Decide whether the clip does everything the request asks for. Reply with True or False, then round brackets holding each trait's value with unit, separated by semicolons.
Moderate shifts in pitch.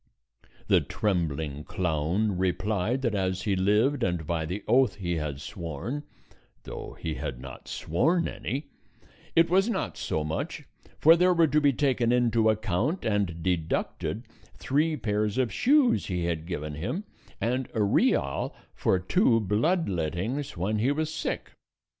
False (7.9 semitones)